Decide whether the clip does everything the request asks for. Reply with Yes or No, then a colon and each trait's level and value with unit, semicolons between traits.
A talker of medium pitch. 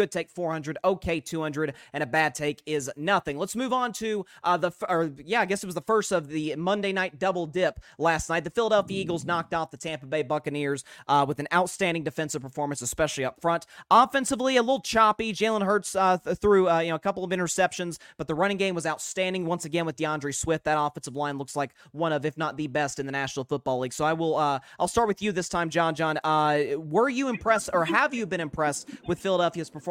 Yes: medium, 165 Hz